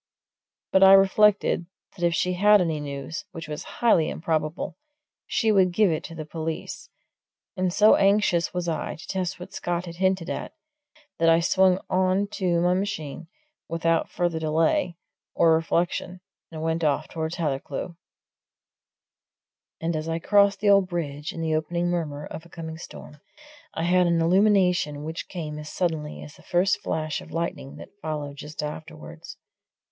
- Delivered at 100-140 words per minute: No, average, 165 wpm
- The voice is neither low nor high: Yes, medium, 170 Hz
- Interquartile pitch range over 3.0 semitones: No, average, 2.7 semitones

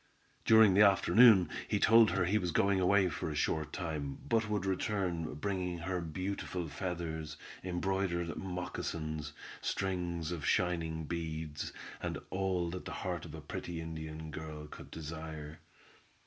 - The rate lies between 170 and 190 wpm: No, average, 145 wpm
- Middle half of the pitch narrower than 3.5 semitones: Yes, average, 3.1 semitones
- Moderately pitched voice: No, very low, 85 Hz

